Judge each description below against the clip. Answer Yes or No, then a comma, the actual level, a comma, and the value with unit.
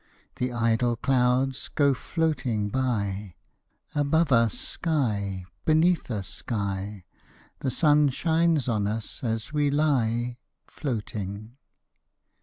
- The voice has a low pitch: Yes, low, 125 Hz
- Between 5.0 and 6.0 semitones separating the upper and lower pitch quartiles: Yes, wide, 5.4 semitones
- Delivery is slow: Yes, slow, 100 wpm